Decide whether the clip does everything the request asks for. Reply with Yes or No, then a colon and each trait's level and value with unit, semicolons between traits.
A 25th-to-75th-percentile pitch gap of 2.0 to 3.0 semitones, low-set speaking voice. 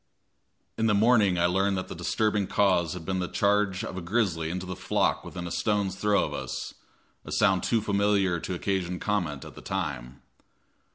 Yes: narrow, 2.5 semitones; very low, 95 Hz